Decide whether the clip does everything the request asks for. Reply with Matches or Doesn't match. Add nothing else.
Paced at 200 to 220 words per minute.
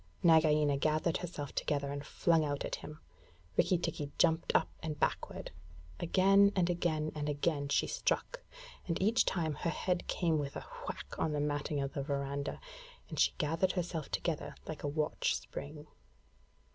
Doesn't match